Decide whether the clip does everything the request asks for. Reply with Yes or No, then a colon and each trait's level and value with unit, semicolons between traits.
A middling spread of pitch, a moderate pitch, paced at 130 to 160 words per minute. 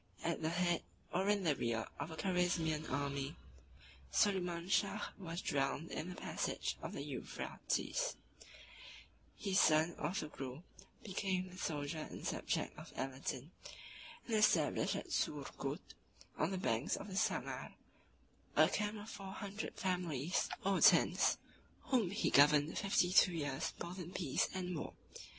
Yes: average, 4.2 semitones; medium, 175 Hz; average, 140 wpm